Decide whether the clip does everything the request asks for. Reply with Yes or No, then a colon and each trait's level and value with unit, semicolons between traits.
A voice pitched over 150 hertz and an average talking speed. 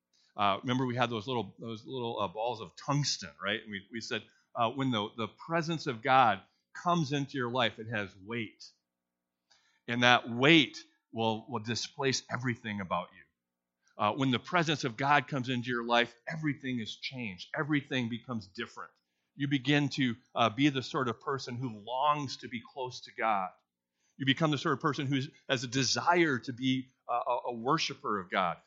No: low, 125 Hz; average, 190 wpm